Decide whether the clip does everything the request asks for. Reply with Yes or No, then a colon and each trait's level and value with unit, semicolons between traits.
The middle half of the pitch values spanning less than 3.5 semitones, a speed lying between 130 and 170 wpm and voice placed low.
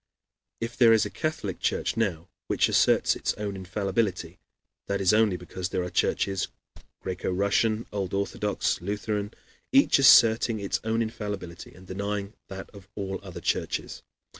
Yes: average, 2.7 semitones; average, 155 wpm; low, 100 Hz